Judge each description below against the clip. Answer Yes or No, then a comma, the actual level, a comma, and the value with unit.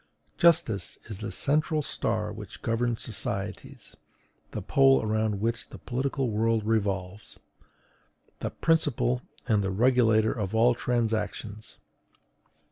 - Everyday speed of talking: No, slow, 115 wpm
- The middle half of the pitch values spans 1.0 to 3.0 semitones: Yes, average, 2.7 semitones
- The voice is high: No, low, 110 Hz